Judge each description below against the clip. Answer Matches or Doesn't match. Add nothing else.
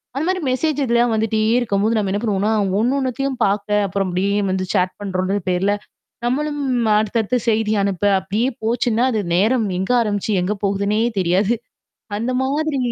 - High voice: Matches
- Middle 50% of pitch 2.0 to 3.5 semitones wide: Doesn't match